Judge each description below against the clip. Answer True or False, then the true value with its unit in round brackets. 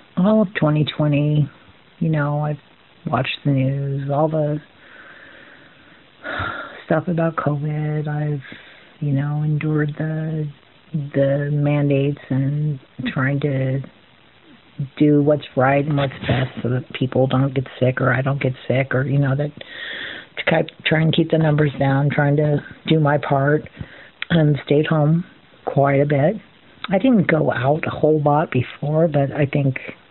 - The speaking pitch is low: False (145 Hz)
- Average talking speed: True (145 wpm)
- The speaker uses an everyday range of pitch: False (1.9 semitones)